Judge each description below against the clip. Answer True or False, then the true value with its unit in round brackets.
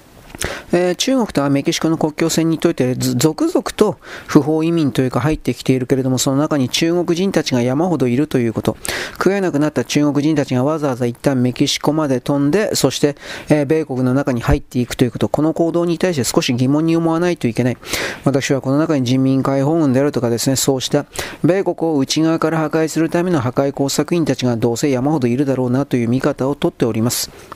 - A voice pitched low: False (145 Hz)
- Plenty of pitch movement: False (3.8 semitones)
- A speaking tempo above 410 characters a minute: True (425 characters per minute)